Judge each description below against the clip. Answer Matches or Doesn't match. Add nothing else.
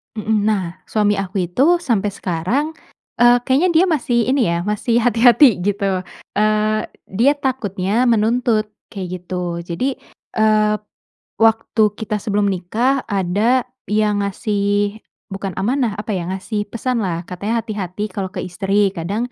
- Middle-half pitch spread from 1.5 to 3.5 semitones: Matches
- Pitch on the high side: Matches